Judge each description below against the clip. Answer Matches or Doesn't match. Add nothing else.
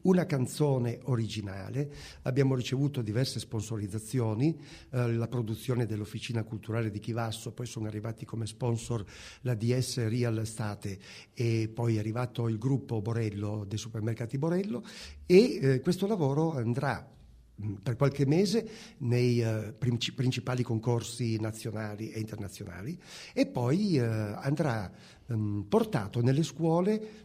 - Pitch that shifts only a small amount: Doesn't match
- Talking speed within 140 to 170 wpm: Doesn't match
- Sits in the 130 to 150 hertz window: Doesn't match